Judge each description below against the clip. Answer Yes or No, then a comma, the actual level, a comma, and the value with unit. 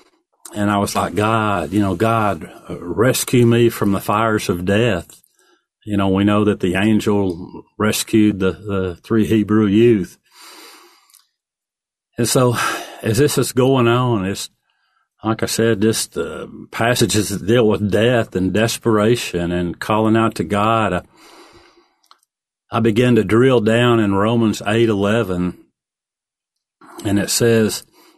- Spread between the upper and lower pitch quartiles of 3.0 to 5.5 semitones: No, narrow, 2.5 semitones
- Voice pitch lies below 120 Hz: Yes, low, 110 Hz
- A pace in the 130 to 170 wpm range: Yes, average, 140 wpm